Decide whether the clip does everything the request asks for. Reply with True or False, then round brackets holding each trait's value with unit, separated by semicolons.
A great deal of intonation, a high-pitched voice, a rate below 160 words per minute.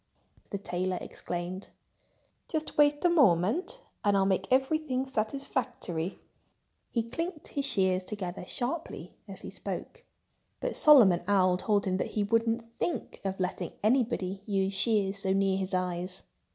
True (6.0 semitones; 205 Hz; 140 wpm)